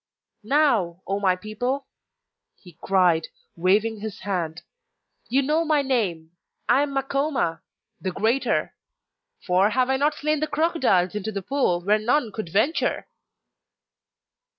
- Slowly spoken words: Yes, slow, 130 wpm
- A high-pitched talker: Yes, high, 215 Hz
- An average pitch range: No, wide, 6.9 semitones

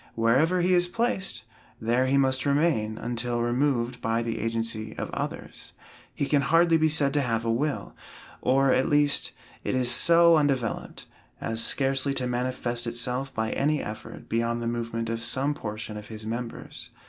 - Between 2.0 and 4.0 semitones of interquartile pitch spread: Yes, average, 3.7 semitones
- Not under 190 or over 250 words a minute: No, average, 170 wpm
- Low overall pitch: Yes, low, 125 Hz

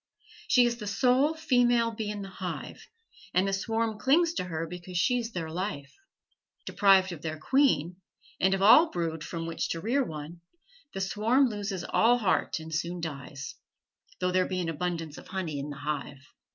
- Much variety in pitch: Yes, wide, 5.7 semitones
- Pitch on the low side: No, medium, 185 Hz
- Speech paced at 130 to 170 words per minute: No, average, 185 wpm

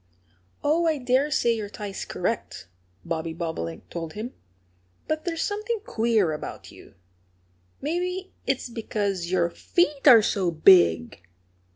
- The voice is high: Yes, high, 220 Hz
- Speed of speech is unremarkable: No, slow, 130 wpm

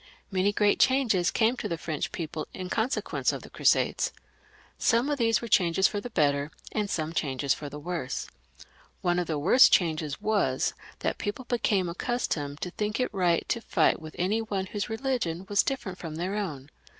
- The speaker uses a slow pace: No, average, 185 wpm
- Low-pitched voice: No, medium, 185 Hz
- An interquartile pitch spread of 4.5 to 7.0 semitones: Yes, wide, 5.6 semitones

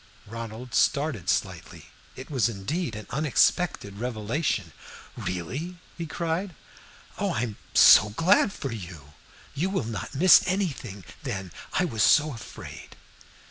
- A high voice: No, low, 125 Hz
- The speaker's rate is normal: No, slow, 130 wpm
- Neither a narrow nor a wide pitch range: No, wide, 7.7 semitones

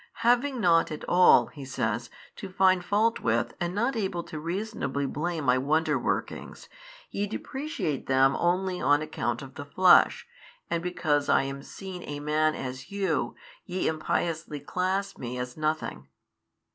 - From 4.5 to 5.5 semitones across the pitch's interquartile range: Yes, average, 4.9 semitones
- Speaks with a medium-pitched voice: Yes, medium, 160 Hz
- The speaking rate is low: No, average, 155 wpm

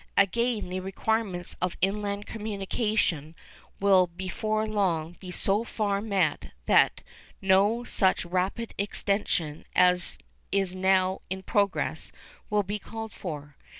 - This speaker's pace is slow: Yes, slow, 115 wpm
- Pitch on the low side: No, high, 195 Hz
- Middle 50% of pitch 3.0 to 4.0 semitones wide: No, narrow, 2.5 semitones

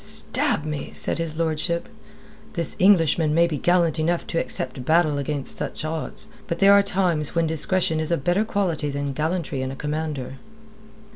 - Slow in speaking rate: No, average, 170 wpm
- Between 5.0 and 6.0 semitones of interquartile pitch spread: No, narrow, 2.5 semitones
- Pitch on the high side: No, medium, 160 Hz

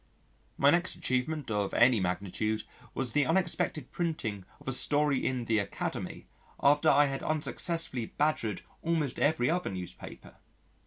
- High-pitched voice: No, low, 135 Hz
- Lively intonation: Yes, wide, 5.8 semitones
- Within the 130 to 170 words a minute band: Yes, average, 140 wpm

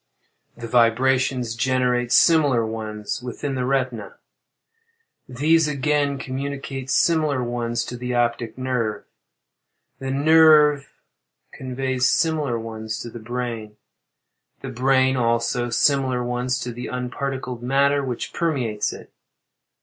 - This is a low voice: Yes, low, 125 Hz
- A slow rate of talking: Yes, slow, 110 wpm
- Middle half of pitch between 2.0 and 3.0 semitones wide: Yes, narrow, 2.6 semitones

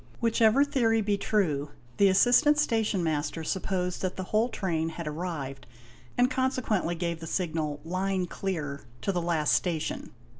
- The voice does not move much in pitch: No, average, 5.2 semitones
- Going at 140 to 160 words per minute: Yes, average, 150 wpm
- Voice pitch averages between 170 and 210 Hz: Yes, medium, 185 Hz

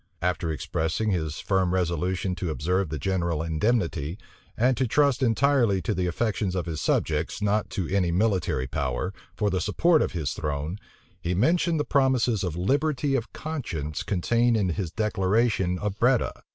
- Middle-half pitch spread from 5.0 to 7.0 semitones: Yes, wide, 5.6 semitones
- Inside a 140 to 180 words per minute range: Yes, average, 165 wpm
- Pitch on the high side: No, very low, 95 Hz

